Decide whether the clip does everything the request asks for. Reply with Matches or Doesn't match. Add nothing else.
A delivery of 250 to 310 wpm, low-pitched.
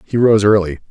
Doesn't match